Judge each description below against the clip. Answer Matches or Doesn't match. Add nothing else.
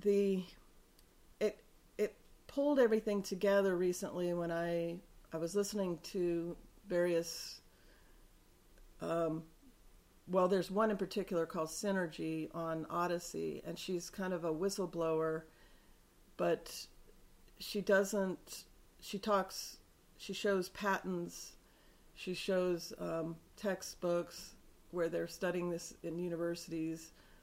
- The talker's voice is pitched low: Doesn't match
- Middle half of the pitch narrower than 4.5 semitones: Matches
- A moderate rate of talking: Doesn't match